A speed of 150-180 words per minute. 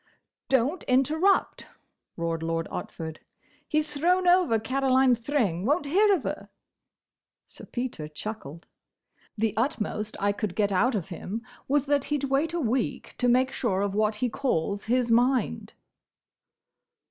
No: average, 140 wpm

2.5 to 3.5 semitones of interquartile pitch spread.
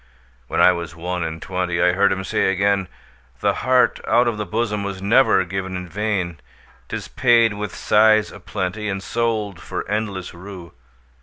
Yes: average, 2.9 semitones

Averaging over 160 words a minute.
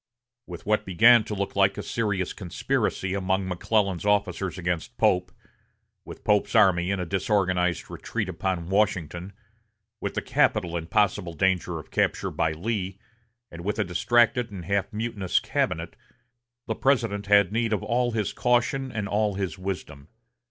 No: average, 155 wpm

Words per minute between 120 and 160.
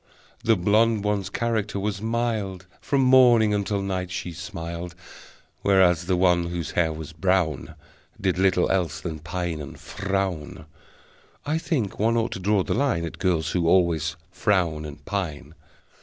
Yes: average, 155 wpm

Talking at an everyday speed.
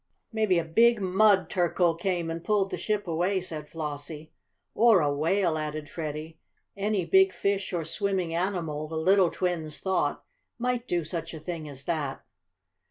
Yes: average, 165 wpm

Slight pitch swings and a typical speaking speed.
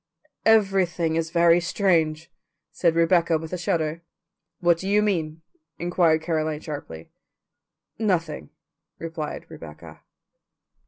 No: narrow, 2.2 semitones; slow, 105 wpm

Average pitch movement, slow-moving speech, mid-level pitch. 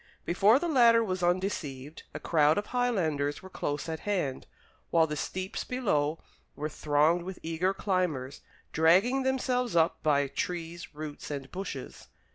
No: average, 4.9 semitones; average, 145 wpm; medium, 170 Hz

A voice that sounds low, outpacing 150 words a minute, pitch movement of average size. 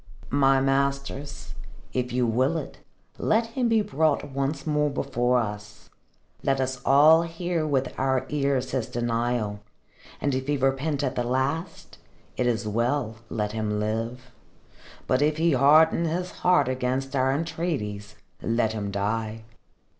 No: low, 130 Hz; average, 145 wpm; average, 3.7 semitones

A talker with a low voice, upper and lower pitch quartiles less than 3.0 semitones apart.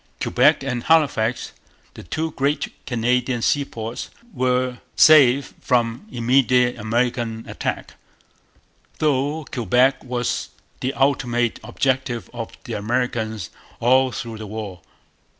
Yes: low, 125 Hz; narrow, 2.4 semitones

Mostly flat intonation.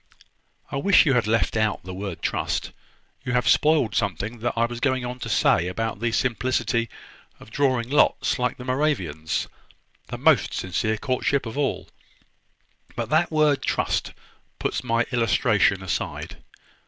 No: average, 3.6 semitones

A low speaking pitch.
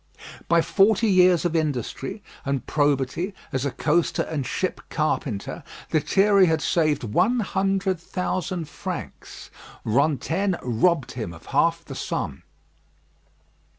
No: medium, 160 Hz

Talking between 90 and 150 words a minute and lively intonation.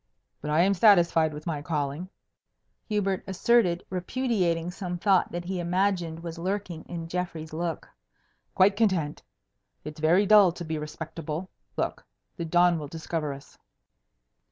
No: average, 140 wpm; average, 2.8 semitones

